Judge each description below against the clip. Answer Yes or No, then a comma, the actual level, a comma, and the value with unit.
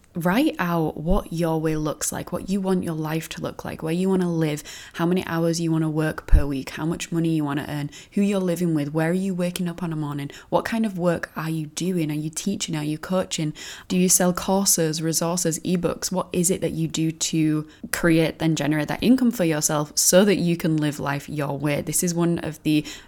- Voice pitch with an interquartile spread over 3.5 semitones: No, narrow, 2.6 semitones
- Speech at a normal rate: No, fast, 245 wpm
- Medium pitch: Yes, medium, 165 Hz